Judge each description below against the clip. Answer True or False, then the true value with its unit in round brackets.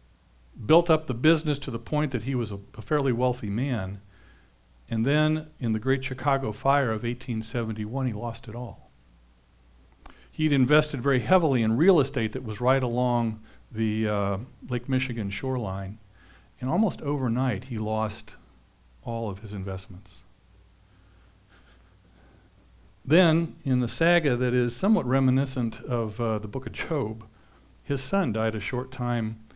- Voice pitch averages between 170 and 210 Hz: False (120 Hz)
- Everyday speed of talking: True (150 wpm)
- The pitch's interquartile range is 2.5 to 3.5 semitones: False (4.6 semitones)